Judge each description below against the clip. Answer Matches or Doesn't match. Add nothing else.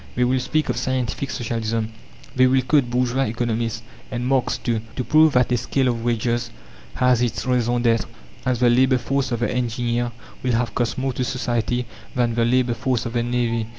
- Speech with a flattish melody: Matches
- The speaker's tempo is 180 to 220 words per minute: Matches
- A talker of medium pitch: Doesn't match